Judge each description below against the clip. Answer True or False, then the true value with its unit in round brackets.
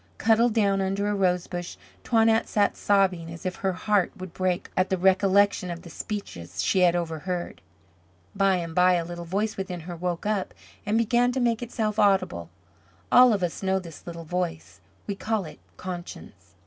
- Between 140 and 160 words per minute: False (180 wpm)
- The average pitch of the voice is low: False (190 Hz)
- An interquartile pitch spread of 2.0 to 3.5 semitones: True (2.9 semitones)